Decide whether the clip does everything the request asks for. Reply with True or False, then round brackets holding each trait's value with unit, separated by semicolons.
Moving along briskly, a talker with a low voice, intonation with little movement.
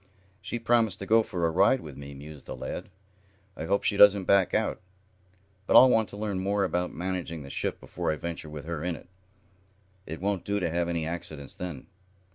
False (210 wpm; 90 Hz; 4.0 semitones)